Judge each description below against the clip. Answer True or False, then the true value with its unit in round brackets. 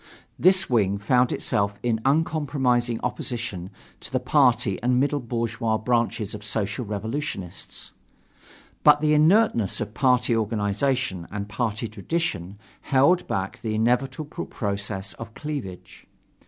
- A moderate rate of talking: False (120 wpm)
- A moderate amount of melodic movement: True (4.7 semitones)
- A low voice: True (120 Hz)